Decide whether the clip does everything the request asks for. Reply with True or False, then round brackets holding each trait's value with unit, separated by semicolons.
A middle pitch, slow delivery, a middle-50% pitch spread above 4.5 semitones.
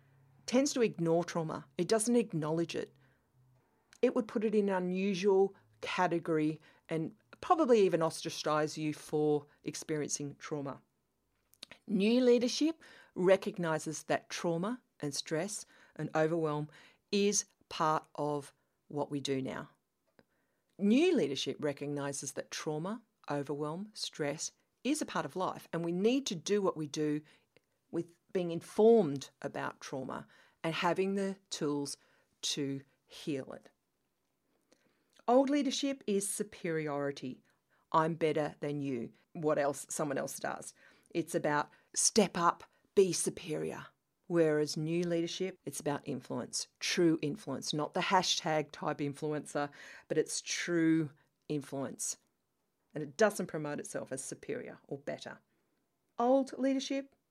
True (165 Hz; 125 wpm; 5.4 semitones)